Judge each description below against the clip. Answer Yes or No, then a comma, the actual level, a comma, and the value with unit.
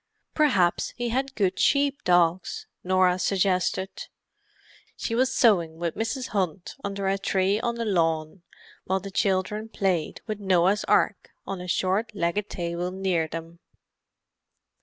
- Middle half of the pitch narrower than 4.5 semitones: Yes, average, 3.3 semitones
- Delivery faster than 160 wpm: No, average, 140 wpm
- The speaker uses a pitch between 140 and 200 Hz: Yes, high, 190 Hz